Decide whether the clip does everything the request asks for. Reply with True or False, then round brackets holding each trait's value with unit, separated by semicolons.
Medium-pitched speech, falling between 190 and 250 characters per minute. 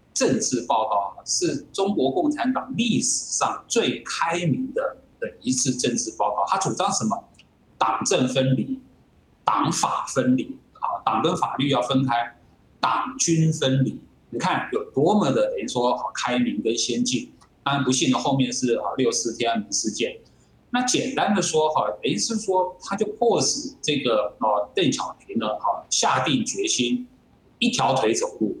True (180 Hz; 230 characters per minute)